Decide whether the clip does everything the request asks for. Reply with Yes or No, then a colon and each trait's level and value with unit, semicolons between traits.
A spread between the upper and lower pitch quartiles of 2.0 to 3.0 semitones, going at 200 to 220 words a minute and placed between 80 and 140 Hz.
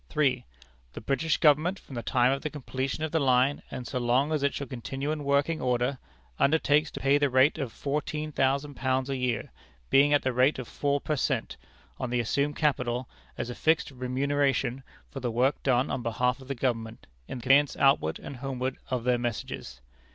Yes: narrow, 2.4 semitones; fast, 205 wpm; low, 135 Hz